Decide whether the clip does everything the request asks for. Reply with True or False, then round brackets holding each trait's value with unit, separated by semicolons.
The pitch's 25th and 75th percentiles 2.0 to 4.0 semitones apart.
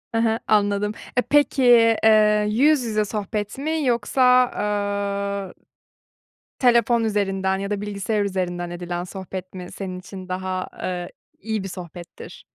True (2.8 semitones)